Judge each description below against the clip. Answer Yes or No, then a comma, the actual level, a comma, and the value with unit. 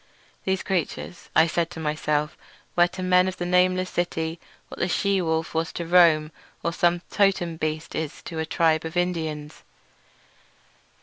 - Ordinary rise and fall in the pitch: No, narrow, 2.2 semitones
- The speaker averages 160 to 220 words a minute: Yes, average, 170 wpm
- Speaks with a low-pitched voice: No, medium, 170 Hz